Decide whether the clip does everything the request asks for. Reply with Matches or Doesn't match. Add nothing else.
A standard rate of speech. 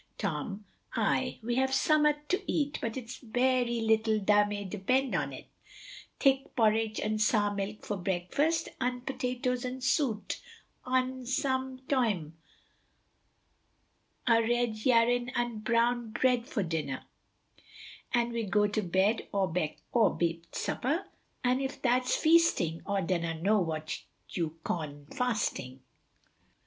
Doesn't match